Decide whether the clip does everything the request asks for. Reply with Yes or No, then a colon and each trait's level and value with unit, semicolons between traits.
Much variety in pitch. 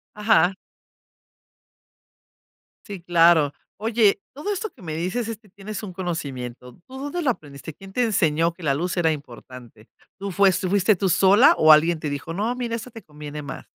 Yes: wide, 5.7 semitones